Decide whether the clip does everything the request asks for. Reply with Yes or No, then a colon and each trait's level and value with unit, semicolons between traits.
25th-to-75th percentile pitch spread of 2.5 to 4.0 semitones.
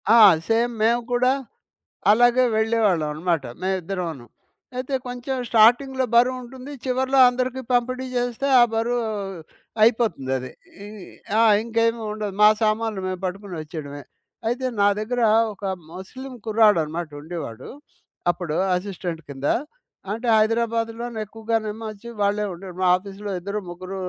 No: average, 4.8 semitones